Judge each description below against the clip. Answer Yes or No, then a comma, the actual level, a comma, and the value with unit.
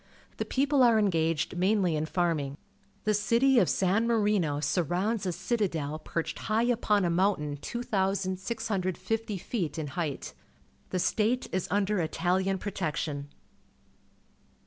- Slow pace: Yes, slow, 125 wpm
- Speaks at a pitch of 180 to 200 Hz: Yes, high, 190 Hz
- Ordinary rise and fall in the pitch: Yes, average, 4.5 semitones